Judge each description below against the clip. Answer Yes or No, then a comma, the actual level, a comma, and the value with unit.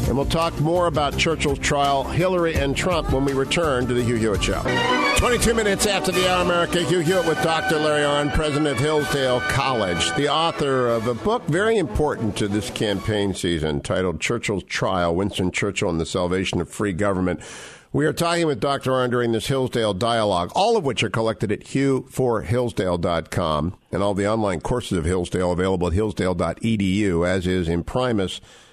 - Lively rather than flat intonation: Yes, wide, 7.5 semitones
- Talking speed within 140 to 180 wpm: No, average, 190 wpm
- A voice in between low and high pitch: No, low, 120 Hz